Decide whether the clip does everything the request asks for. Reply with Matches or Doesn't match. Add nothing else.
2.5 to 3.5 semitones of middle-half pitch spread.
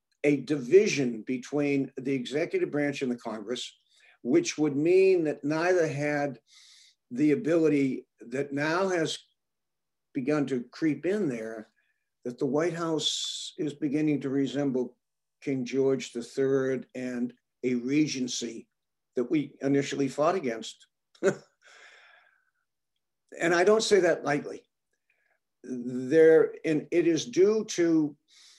Doesn't match